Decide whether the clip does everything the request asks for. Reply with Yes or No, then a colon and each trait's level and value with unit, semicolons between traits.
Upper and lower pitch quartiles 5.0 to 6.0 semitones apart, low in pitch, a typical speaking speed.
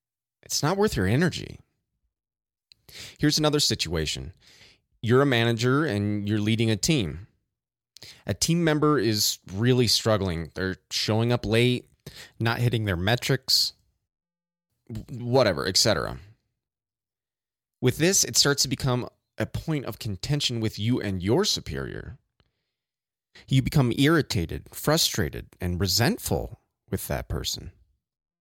No: wide, 5.4 semitones; low, 115 Hz; slow, 120 wpm